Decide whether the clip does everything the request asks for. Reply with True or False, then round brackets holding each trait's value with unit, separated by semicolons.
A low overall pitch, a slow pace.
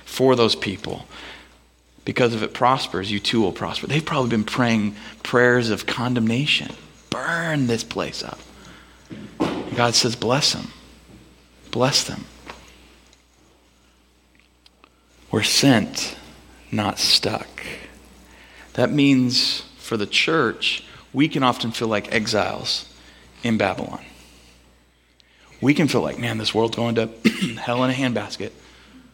True (110 Hz; 120 wpm)